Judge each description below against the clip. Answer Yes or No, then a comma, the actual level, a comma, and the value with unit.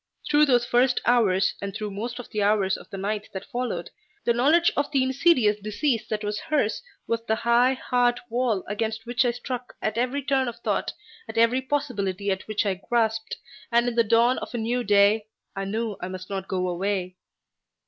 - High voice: Yes, high, 225 Hz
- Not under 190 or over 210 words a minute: Yes, average, 200 wpm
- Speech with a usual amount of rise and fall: Yes, average, 3.3 semitones